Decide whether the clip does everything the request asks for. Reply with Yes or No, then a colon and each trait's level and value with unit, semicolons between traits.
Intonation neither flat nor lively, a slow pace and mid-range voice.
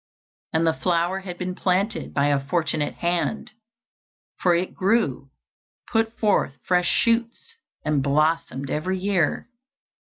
Yes: average, 4.2 semitones; slow, 125 wpm; medium, 175 Hz